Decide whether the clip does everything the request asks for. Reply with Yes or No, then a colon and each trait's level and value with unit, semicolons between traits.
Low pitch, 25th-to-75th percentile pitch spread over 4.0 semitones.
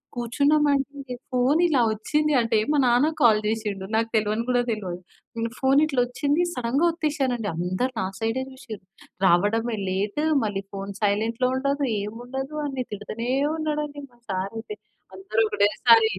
No: high, 240 Hz; average, 4.5 semitones